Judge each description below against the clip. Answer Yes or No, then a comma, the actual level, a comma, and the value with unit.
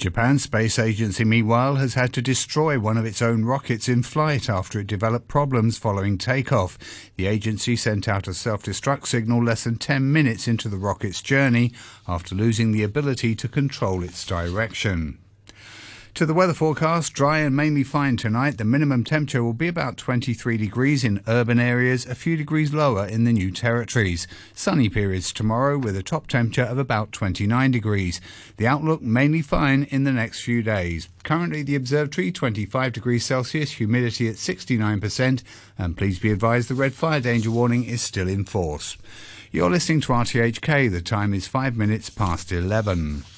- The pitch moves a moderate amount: Yes, average, 4.2 semitones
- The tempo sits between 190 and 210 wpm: No, average, 175 wpm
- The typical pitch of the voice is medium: No, low, 115 Hz